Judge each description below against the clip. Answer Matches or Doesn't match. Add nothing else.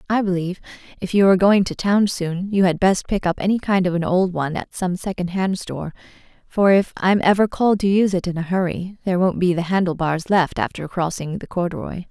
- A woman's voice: Matches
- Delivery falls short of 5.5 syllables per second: Doesn't match